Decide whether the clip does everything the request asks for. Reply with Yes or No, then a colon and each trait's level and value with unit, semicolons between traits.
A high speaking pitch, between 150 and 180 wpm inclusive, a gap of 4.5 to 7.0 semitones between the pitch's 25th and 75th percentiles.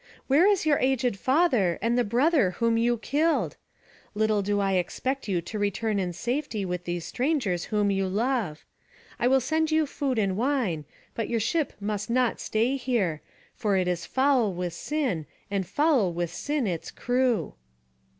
Yes: high, 230 Hz; average, 170 wpm; wide, 5.6 semitones